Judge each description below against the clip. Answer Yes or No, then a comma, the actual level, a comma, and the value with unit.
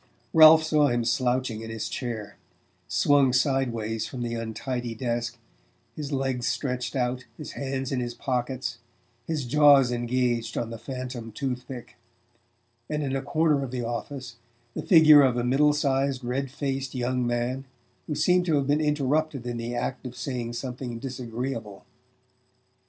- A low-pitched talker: Yes, low, 130 Hz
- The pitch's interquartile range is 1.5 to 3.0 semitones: Yes, narrow, 2.5 semitones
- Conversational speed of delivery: Yes, average, 155 wpm